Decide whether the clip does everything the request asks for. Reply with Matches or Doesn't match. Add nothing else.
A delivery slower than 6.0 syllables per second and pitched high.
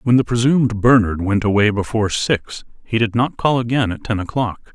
Doesn't match